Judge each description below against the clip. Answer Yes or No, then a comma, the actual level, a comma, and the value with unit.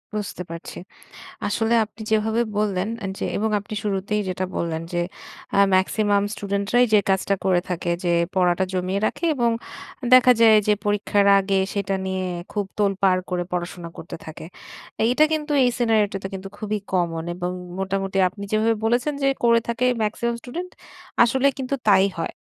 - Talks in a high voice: Yes, high, 200 Hz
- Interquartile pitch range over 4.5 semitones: No, average, 3.3 semitones